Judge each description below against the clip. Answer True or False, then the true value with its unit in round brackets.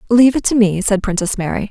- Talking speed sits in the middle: False (245 wpm)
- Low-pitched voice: False (210 Hz)